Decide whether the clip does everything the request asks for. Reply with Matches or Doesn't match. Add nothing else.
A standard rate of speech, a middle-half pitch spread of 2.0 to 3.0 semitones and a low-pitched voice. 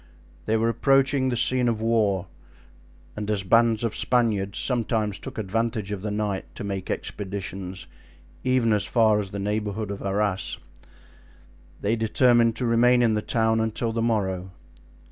Matches